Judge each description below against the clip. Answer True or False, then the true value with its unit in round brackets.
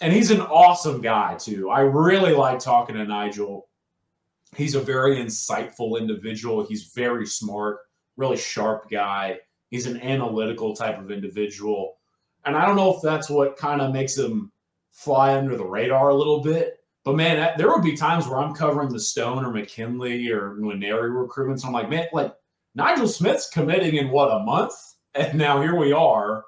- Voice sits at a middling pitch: False (130 Hz)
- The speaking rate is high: False (180 wpm)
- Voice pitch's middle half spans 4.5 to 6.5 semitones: True (5.5 semitones)